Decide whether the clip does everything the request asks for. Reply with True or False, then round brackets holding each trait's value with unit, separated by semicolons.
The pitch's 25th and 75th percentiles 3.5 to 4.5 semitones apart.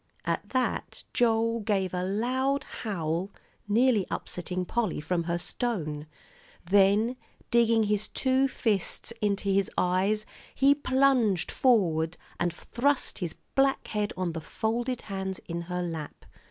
False (5.0 semitones)